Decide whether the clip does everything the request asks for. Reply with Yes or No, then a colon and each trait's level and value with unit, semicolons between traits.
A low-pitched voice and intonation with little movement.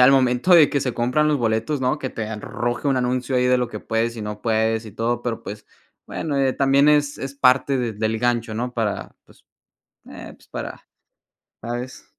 No: low, 125 Hz; average, 3.1 semitones